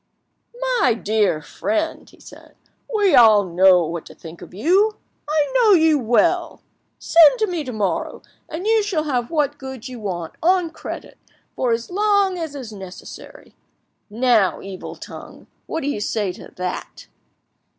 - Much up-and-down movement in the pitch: Yes, wide, 8.4 semitones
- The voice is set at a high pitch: Yes, very high, 260 Hz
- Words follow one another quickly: No, average, 155 wpm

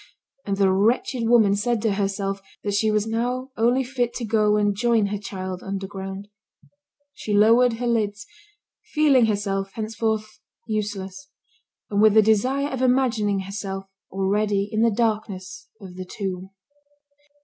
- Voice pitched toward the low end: No, high, 210 Hz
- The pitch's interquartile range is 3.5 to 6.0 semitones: No, average, 2.7 semitones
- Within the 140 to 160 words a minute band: Yes, average, 145 wpm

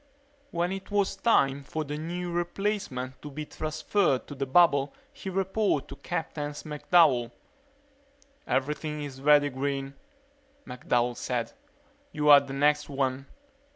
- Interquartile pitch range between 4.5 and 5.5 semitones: No, average, 4.1 semitones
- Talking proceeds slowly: Yes, slow, 130 wpm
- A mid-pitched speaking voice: Yes, medium, 150 Hz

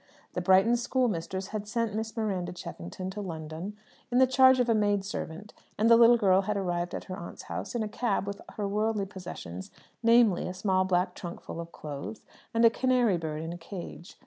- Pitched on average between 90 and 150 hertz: No, high, 200 Hz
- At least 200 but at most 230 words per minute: Yes, fast, 205 wpm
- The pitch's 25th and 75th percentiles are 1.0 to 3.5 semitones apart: No, average, 4.1 semitones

